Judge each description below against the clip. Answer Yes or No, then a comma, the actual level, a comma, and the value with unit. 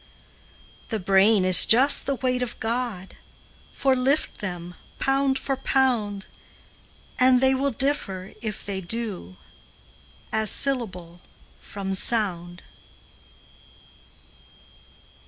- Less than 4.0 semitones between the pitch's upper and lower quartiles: No, wide, 5.5 semitones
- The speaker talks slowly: Yes, slow, 100 wpm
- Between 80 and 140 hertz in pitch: No, high, 225 Hz